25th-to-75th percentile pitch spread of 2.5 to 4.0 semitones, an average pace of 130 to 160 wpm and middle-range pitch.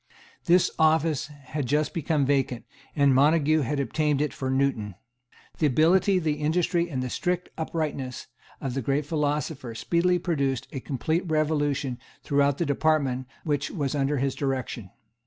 Yes: average, 2.8 semitones; average, 150 wpm; medium, 145 Hz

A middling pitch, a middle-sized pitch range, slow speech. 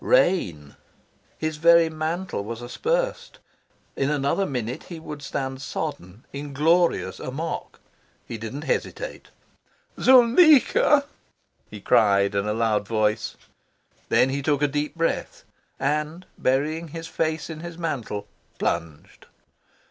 No: medium, 145 Hz; wide, 6.2 semitones; slow, 120 wpm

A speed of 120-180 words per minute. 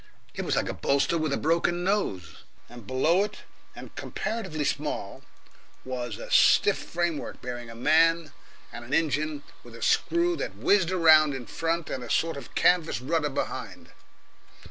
Yes: average, 165 wpm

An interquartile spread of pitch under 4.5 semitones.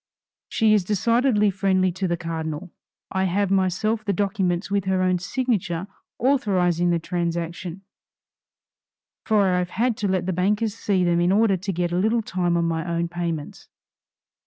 Yes: average, 2.8 semitones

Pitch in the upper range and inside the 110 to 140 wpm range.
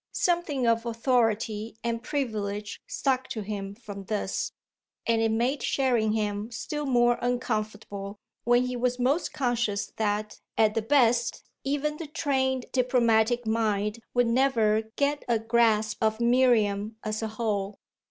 Yes: high, 230 Hz; slow, 135 wpm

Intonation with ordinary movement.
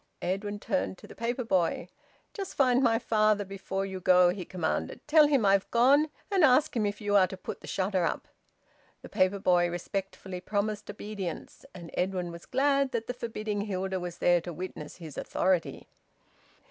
Yes: average, 4.0 semitones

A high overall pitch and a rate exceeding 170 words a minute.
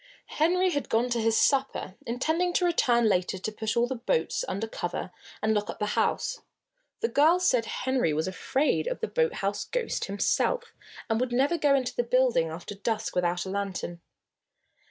Yes: high, 240 Hz; average, 180 wpm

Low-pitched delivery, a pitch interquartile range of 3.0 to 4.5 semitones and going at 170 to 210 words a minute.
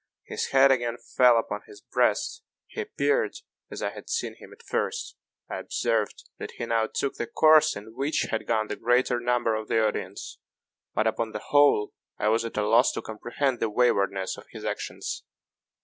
Yes: low, 120 Hz; average, 3.6 semitones; average, 190 wpm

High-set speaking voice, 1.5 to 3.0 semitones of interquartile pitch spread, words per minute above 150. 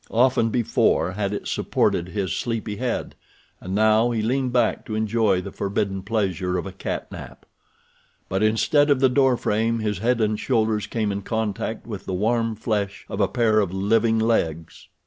No: low, 110 Hz; narrow, 2.6 semitones; average, 180 wpm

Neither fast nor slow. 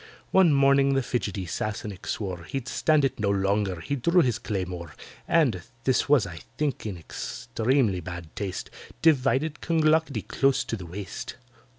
Yes: average, 150 wpm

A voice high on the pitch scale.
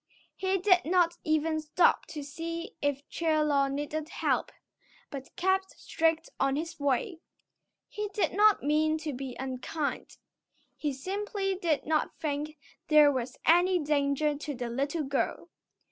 Yes: very high, 310 Hz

